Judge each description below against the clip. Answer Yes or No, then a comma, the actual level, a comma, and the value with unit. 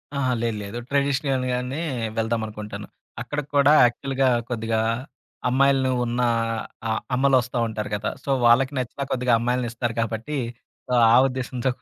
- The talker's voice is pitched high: No, low, 125 Hz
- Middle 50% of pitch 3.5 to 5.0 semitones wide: No, average, 2.7 semitones